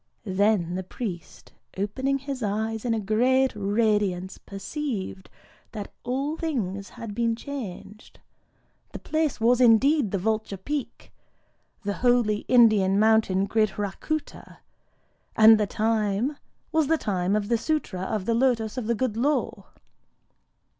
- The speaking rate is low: Yes, slow, 125 wpm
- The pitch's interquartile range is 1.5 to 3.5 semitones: No, average, 4.1 semitones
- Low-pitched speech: No, high, 220 Hz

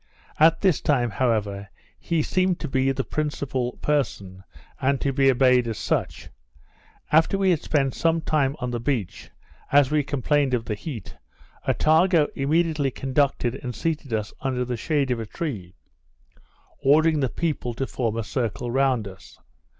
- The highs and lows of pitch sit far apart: No, average, 4.0 semitones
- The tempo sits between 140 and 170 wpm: Yes, average, 160 wpm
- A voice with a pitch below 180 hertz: Yes, low, 135 Hz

